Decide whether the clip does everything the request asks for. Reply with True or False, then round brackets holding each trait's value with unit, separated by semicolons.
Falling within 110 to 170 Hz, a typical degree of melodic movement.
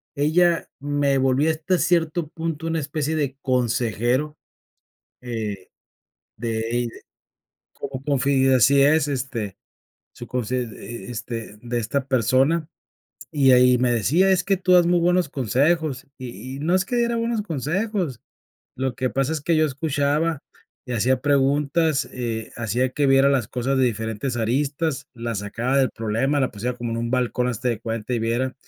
True (135 Hz; 4.3 semitones)